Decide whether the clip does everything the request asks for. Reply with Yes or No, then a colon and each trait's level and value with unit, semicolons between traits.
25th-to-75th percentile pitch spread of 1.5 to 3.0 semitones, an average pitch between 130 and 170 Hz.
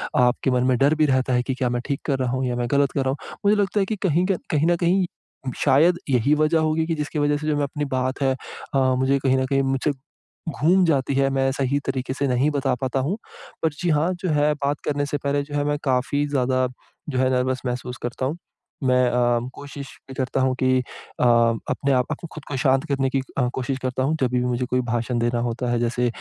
Yes: narrow, 2.5 semitones; low, 135 Hz